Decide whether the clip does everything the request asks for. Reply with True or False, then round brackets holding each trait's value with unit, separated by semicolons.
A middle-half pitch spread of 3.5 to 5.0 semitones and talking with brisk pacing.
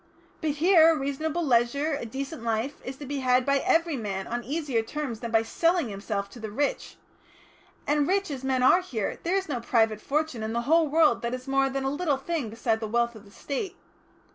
True (4.7 semitones; 220 wpm)